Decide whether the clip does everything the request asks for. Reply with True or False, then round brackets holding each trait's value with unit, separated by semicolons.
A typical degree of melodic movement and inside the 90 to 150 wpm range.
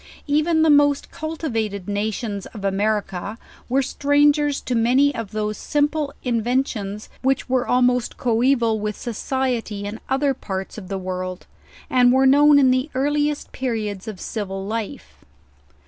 True (4.9 semitones; 145 wpm)